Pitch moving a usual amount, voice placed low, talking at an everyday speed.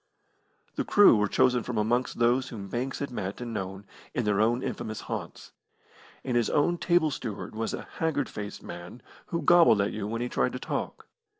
Yes: average, 4.1 semitones; low, 120 Hz; average, 195 wpm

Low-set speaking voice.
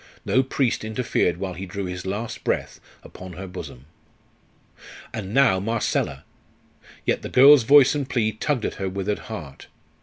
Yes: low, 105 Hz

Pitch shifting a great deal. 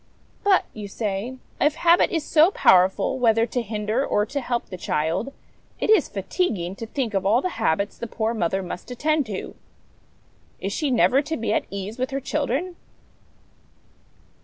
Yes: wide, 5.8 semitones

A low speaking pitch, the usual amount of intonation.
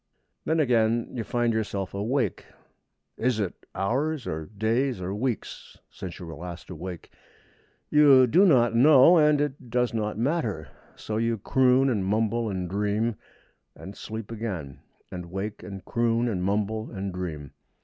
Yes: low, 110 Hz; average, 4.4 semitones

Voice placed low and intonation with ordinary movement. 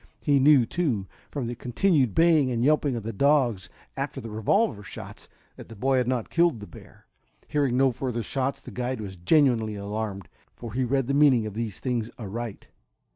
Yes: low, 125 Hz; average, 4.0 semitones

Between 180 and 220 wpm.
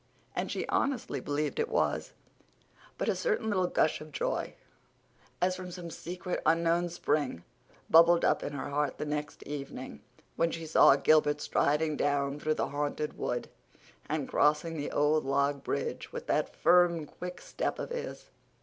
No: average, 160 wpm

